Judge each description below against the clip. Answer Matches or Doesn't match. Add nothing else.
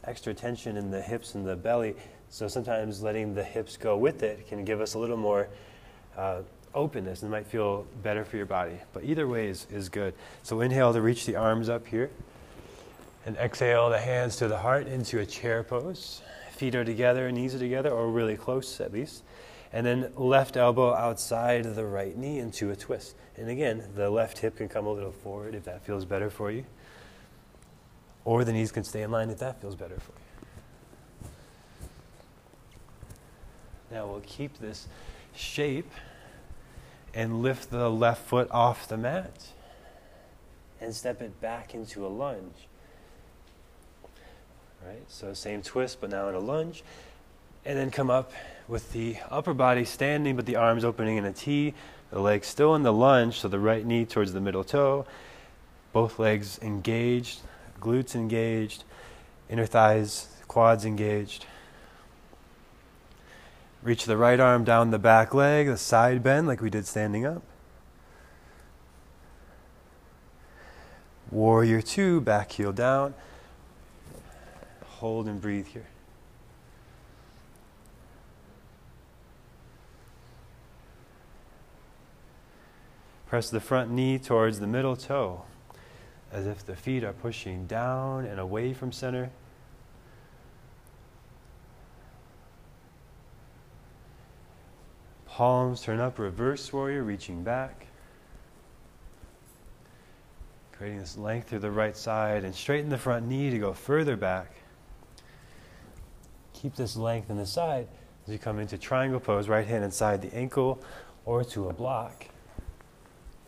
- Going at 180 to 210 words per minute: Doesn't match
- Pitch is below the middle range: Matches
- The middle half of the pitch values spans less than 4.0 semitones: Matches